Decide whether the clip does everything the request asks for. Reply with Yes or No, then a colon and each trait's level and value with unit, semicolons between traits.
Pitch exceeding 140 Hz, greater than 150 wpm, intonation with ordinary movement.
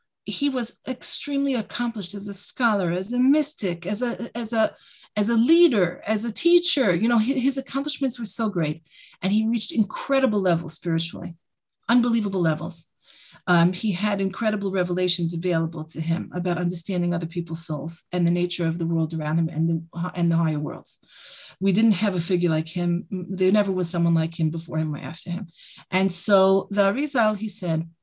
Yes: medium, 185 Hz; average, 185 wpm; average, 4.9 semitones